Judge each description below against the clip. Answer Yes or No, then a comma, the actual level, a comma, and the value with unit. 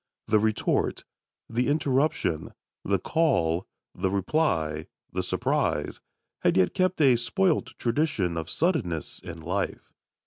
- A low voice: Yes, low, 110 Hz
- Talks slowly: Yes, slow, 115 wpm